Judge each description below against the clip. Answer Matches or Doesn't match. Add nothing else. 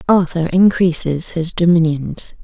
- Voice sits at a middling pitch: Matches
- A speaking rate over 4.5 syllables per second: Doesn't match